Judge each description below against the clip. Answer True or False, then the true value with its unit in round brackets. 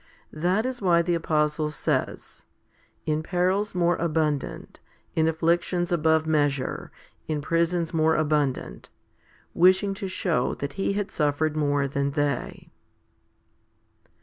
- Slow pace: True (120 wpm)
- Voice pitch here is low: False (160 Hz)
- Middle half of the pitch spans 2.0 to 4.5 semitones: True (2.8 semitones)